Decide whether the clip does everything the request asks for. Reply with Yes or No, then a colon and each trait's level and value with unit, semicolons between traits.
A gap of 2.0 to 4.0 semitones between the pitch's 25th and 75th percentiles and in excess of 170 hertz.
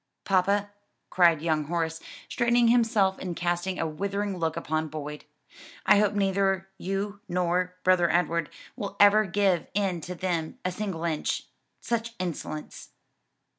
Yes: average, 3.2 semitones; medium, 185 Hz